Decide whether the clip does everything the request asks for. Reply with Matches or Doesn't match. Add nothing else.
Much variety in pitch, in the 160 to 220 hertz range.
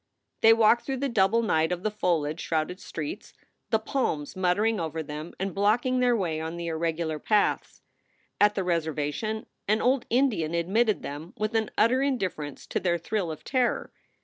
Matches